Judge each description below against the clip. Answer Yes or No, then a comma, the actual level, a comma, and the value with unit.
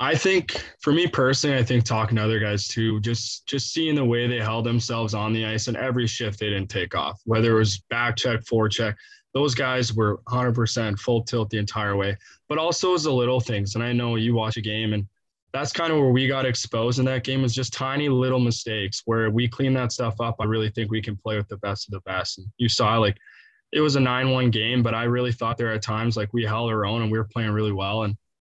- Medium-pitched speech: No, low, 115 Hz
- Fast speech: Yes, fast, 260 wpm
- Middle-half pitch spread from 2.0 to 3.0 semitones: Yes, average, 2.7 semitones